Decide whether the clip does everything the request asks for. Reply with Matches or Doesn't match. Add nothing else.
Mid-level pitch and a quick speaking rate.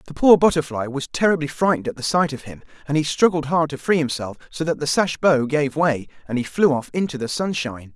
Matches